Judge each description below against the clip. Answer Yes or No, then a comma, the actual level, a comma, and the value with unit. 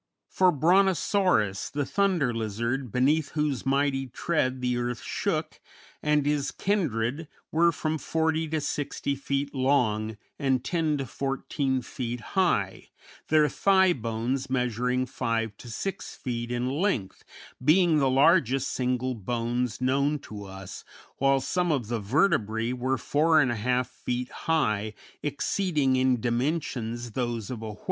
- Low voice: Yes, low, 130 Hz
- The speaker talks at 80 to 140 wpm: Yes, slow, 135 wpm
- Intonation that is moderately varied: Yes, average, 4.1 semitones